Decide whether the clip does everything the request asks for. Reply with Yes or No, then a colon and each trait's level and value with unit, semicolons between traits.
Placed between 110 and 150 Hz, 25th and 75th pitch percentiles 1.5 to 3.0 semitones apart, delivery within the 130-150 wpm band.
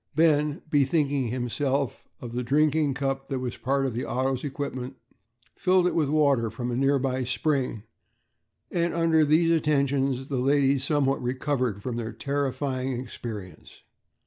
Yes: low, 135 Hz; narrow, 2.5 semitones; average, 145 wpm